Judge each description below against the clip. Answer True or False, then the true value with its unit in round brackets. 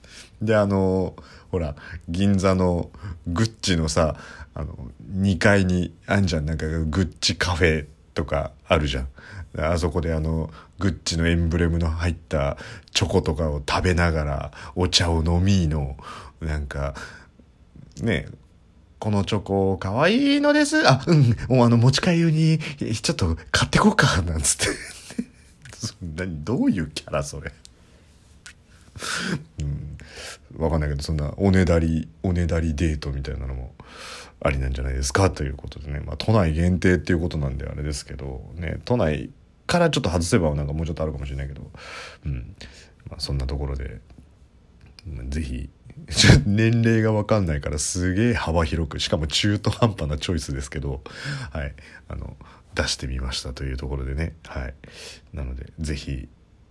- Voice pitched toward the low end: True (85 Hz)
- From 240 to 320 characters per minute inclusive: True (315 characters per minute)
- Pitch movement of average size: True (4.6 semitones)